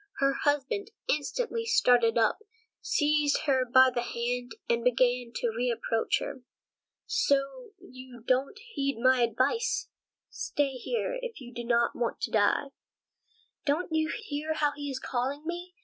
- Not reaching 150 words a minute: Yes, average, 140 wpm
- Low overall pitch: No, very high, 270 Hz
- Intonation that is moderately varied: Yes, average, 4.2 semitones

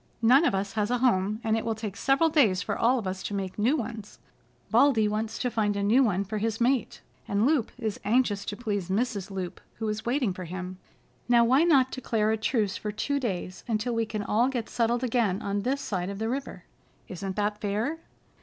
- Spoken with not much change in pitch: No, average, 3.4 semitones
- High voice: Yes, high, 220 Hz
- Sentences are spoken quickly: Yes, fast, 220 wpm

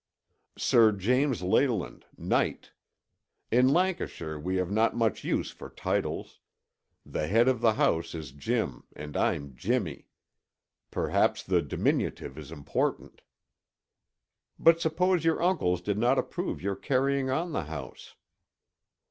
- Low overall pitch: Yes, low, 115 Hz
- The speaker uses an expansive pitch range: Yes, wide, 8.6 semitones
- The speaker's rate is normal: No, slow, 125 wpm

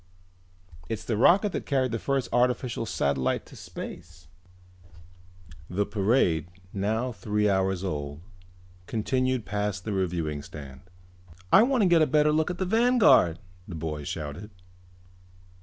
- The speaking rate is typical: No, slow, 130 wpm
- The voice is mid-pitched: No, low, 105 Hz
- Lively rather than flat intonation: Yes, wide, 7.9 semitones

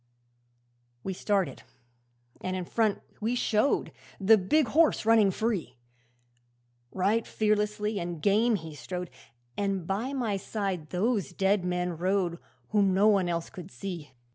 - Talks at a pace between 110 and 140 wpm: Yes, slow, 135 wpm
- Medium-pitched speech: No, high, 195 Hz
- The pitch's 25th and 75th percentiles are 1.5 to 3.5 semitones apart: Yes, average, 3.2 semitones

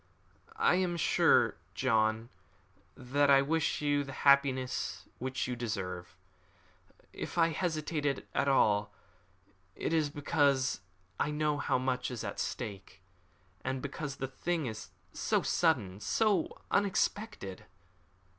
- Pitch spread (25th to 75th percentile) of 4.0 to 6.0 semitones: Yes, average, 4.4 semitones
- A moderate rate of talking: No, slow, 120 wpm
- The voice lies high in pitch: No, low, 135 Hz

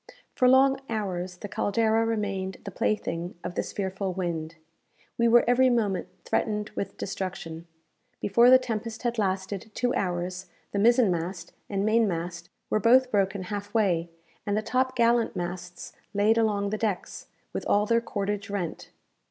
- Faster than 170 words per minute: No, average, 160 wpm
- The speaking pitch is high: Yes, high, 205 Hz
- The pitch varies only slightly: No, average, 3.7 semitones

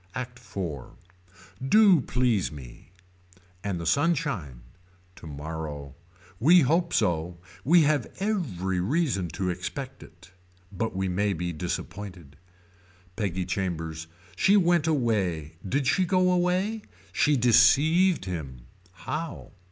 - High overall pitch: No, low, 105 Hz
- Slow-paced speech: Yes, slow, 115 wpm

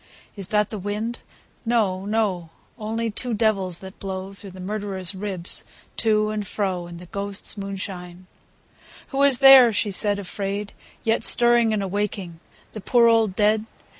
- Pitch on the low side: No, high, 205 Hz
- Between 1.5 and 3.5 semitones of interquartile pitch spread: Yes, average, 2.7 semitones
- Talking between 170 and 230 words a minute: No, average, 160 wpm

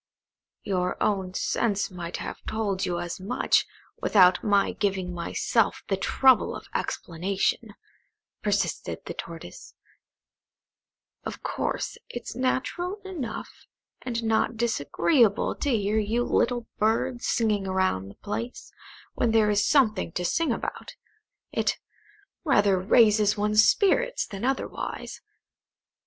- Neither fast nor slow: No, slow, 115 wpm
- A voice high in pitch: Yes, high, 210 Hz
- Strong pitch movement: No, average, 3.9 semitones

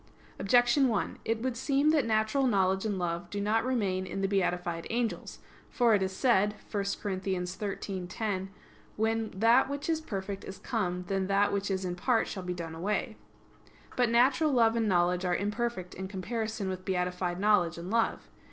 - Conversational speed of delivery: Yes, average, 180 wpm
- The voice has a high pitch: Yes, high, 200 Hz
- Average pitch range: Yes, average, 3.6 semitones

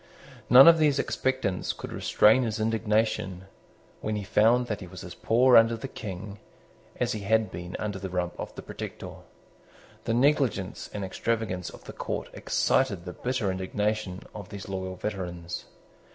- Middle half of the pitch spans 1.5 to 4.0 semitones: Yes, average, 3.6 semitones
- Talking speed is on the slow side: No, average, 165 wpm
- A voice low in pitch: Yes, low, 105 Hz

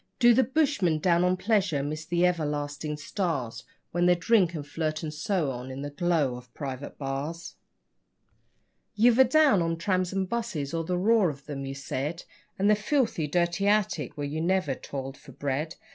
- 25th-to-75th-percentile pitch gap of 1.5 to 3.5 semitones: No, average, 4.9 semitones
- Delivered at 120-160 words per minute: No, average, 185 wpm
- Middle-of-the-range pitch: Yes, medium, 165 Hz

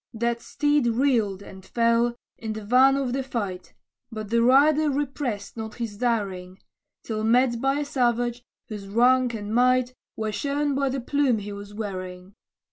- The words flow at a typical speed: Yes, average, 165 wpm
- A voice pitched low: No, high, 235 Hz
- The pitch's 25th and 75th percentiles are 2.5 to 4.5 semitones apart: Yes, average, 3.9 semitones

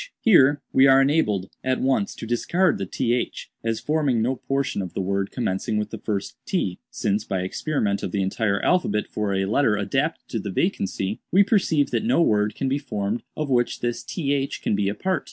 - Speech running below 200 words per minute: No, fast, 205 wpm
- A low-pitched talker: Yes, low, 115 Hz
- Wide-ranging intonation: Yes, wide, 5.9 semitones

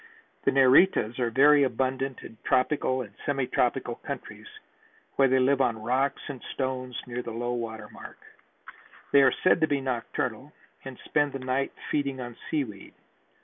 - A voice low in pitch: Yes, low, 130 Hz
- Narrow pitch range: Yes, narrow, 2.2 semitones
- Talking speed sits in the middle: Yes, average, 155 wpm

